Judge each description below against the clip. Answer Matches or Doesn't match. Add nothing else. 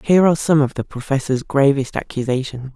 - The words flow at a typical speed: Matches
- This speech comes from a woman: Matches